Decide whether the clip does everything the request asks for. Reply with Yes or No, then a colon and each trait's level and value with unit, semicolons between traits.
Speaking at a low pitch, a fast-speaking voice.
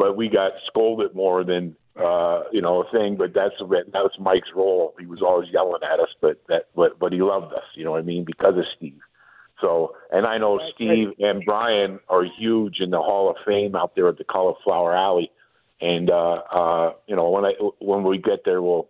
Yes: low, 105 Hz; fast, 220 wpm